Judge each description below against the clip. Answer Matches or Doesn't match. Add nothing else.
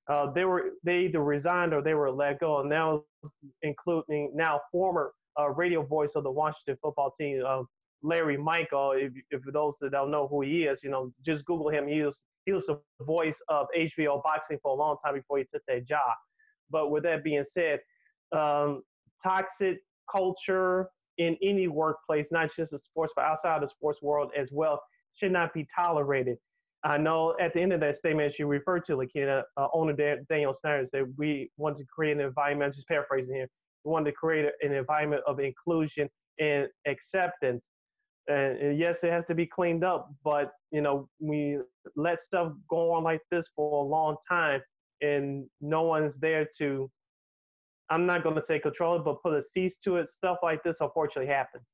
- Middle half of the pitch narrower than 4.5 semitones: Matches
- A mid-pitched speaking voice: Matches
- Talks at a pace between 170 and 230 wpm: Matches